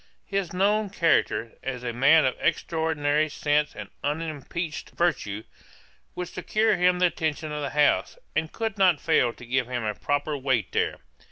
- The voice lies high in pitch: No, medium, 150 Hz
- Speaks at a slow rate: No, average, 165 wpm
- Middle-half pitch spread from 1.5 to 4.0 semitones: No, average, 4.9 semitones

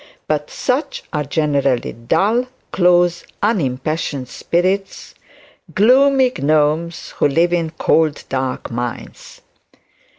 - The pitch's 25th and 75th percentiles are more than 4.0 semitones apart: Yes, average, 5.2 semitones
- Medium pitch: Yes, medium, 160 Hz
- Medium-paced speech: No, slow, 95 wpm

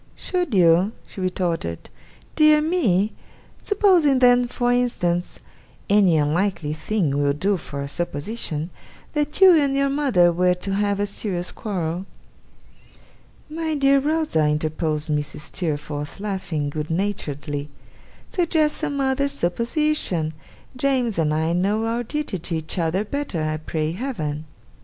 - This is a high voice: Yes, high, 195 Hz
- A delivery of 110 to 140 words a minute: Yes, slow, 135 wpm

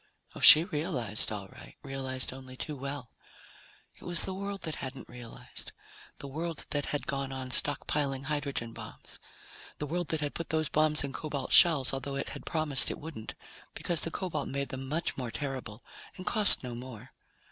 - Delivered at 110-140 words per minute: No, average, 180 wpm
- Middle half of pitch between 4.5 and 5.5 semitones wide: No, average, 3.1 semitones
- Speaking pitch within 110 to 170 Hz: Yes, medium, 140 Hz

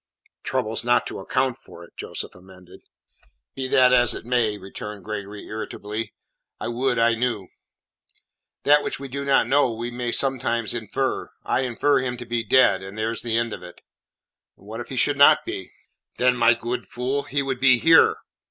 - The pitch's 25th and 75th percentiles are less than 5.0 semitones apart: Yes, average, 3.1 semitones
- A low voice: Yes, low, 120 Hz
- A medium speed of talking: Yes, average, 180 wpm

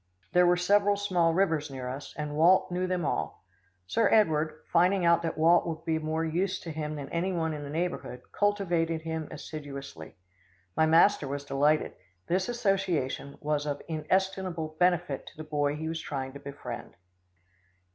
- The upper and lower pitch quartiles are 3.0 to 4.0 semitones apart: Yes, average, 3.3 semitones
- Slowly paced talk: No, average, 175 wpm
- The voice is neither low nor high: Yes, medium, 160 Hz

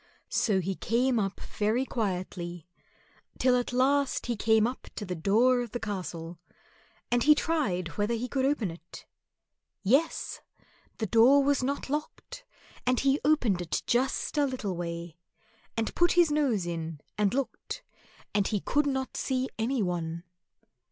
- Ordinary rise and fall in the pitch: No, wide, 6.2 semitones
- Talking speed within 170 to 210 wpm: No, average, 155 wpm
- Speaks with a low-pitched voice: No, high, 235 Hz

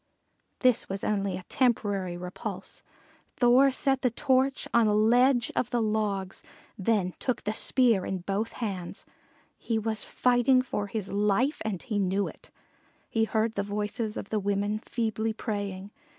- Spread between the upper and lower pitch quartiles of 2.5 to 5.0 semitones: Yes, average, 3.3 semitones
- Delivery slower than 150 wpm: No, average, 155 wpm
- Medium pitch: No, high, 215 Hz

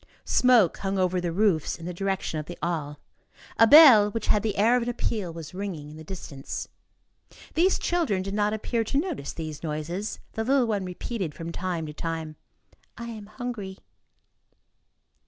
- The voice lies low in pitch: No, high, 195 Hz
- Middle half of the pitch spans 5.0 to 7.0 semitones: Yes, average, 5.3 semitones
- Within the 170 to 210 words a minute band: Yes, average, 175 wpm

